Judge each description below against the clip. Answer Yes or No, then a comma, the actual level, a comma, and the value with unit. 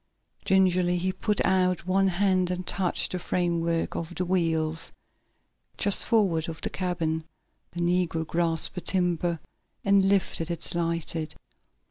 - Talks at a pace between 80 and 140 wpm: Yes, slow, 135 wpm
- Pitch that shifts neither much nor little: No, narrow, 2.0 semitones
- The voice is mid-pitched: Yes, medium, 175 Hz